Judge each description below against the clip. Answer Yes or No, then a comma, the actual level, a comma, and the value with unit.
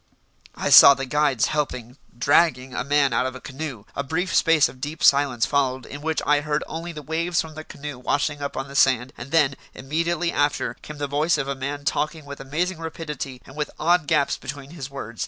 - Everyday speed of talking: No, fast, 215 wpm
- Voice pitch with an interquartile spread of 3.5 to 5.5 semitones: No, average, 2.8 semitones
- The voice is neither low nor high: Yes, medium, 145 Hz